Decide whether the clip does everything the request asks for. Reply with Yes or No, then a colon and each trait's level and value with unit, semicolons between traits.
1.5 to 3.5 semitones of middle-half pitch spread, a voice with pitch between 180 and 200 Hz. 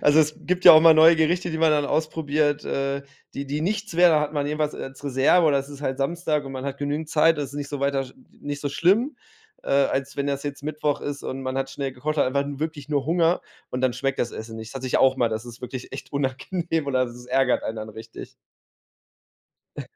No: average, 2.7 semitones; medium, 145 Hz